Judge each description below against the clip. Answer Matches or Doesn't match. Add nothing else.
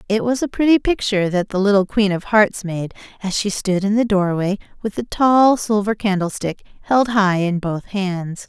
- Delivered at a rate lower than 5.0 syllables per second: Matches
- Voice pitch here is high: Matches